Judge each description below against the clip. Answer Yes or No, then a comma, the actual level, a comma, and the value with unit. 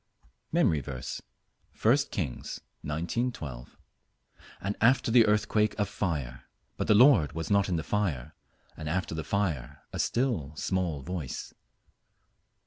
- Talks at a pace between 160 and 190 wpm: No, slow, 135 wpm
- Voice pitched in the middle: No, very low, 90 Hz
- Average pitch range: No, wide, 6.0 semitones